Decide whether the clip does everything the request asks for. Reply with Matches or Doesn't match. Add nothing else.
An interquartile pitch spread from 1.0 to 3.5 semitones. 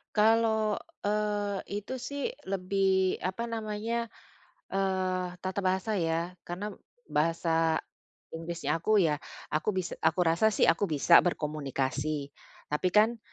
Doesn't match